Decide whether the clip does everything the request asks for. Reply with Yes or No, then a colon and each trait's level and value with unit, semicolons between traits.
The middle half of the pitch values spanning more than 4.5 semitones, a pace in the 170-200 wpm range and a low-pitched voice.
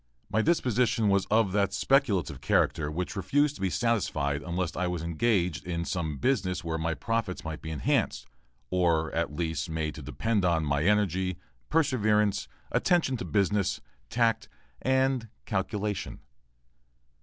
No: wide, 5.4 semitones; average, 145 wpm; very low, 95 Hz